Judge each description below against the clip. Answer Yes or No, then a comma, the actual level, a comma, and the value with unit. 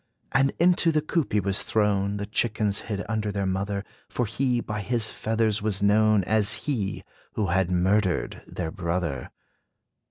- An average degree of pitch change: No, narrow, 2.3 semitones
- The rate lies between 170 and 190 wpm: No, average, 160 wpm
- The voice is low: Yes, low, 105 Hz